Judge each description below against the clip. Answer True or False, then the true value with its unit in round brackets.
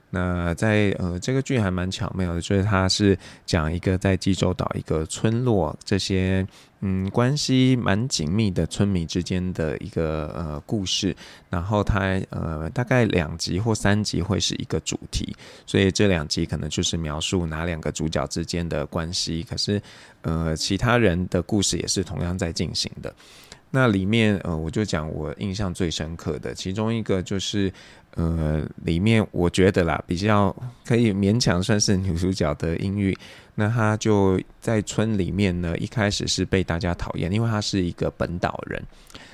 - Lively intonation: False (3.6 semitones)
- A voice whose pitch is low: True (95 Hz)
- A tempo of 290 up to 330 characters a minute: False (255 characters per minute)